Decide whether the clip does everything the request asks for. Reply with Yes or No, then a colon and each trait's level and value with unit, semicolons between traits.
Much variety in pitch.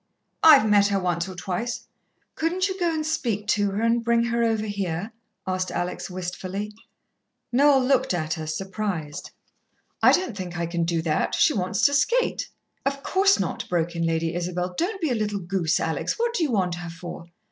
Yes: wide, 5.8 semitones